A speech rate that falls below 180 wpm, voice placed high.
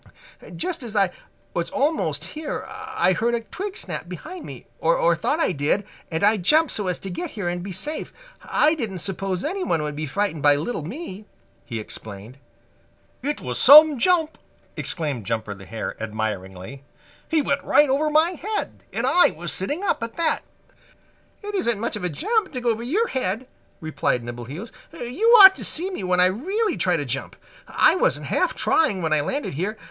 No: average, 190 wpm; high, 210 Hz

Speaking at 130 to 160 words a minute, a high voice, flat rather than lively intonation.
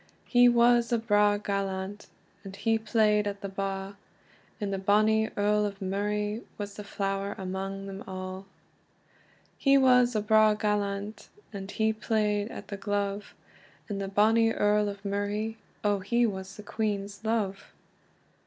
Yes: average, 150 wpm; high, 205 Hz; narrow, 1.7 semitones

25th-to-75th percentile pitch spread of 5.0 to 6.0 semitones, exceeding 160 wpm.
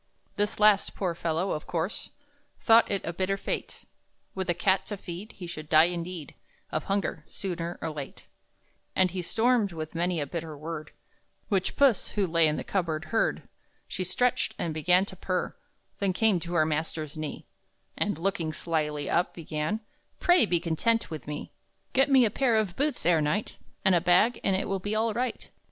No: average, 4.2 semitones; average, 185 wpm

